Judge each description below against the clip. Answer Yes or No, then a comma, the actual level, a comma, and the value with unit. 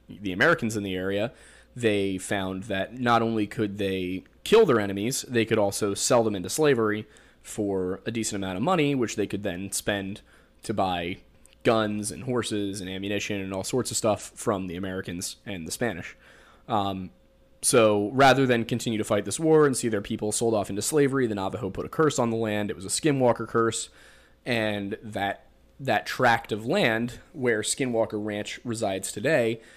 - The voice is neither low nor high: No, low, 105 Hz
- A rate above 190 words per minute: No, average, 185 wpm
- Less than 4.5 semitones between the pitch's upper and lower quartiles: Yes, average, 3.0 semitones